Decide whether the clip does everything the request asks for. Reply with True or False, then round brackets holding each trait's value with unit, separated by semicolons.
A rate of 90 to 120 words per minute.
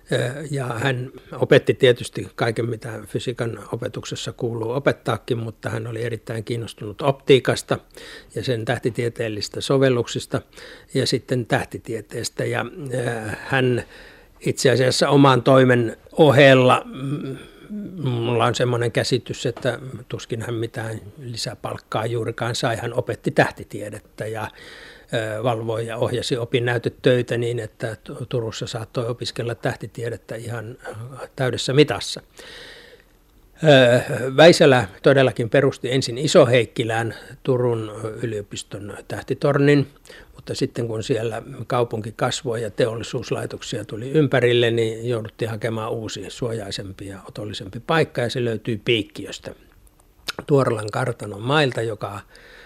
True (105 wpm)